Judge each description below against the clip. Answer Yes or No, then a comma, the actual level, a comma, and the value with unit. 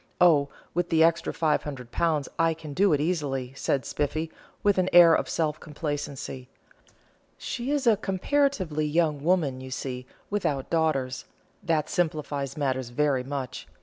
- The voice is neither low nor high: Yes, medium, 155 Hz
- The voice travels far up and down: No, average, 3.7 semitones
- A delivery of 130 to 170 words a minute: Yes, average, 145 wpm